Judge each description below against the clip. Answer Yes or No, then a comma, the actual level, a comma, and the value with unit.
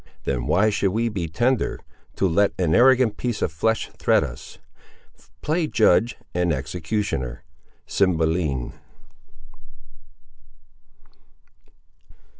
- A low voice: Yes, very low, 95 Hz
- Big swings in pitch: Yes, wide, 5.8 semitones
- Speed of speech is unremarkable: No, slow, 95 wpm